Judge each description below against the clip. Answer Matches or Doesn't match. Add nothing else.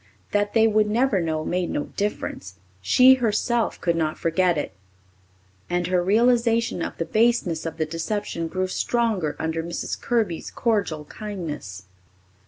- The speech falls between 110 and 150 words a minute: Matches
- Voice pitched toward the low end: Doesn't match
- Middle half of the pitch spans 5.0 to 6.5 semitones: Matches